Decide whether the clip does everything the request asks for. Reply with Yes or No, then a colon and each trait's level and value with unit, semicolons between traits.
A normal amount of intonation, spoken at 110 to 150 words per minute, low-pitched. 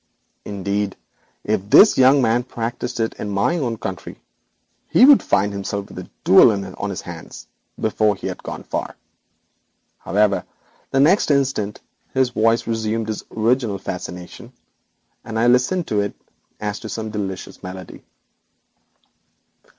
Yes: average, 3.5 semitones; average, 145 wpm; low, 110 Hz